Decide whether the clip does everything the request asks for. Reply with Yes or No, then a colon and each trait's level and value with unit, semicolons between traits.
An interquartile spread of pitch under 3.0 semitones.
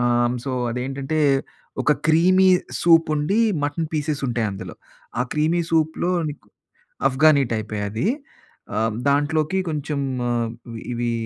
No: average, 4.8 semitones